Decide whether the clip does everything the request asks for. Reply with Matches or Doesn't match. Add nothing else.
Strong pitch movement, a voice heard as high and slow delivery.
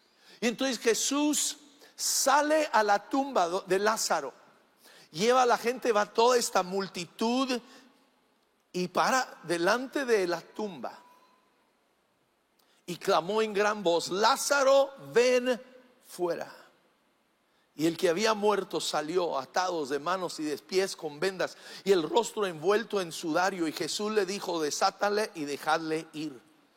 Matches